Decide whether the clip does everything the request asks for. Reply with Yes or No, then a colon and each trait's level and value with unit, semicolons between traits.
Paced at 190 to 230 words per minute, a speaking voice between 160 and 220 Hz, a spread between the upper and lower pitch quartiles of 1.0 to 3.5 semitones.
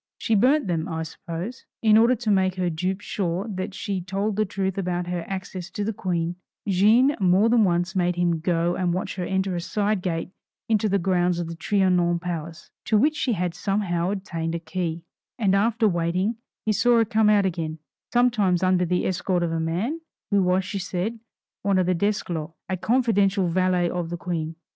Yes: average, 195 wpm; medium, 185 Hz; average, 3.0 semitones